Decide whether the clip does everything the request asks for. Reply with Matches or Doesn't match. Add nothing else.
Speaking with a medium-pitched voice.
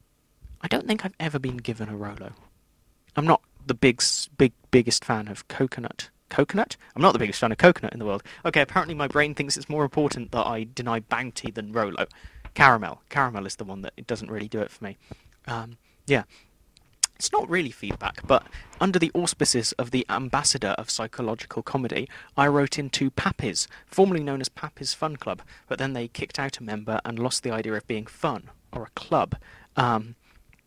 Doesn't match